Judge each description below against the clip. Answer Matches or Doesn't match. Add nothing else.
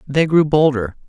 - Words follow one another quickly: Doesn't match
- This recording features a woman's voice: Doesn't match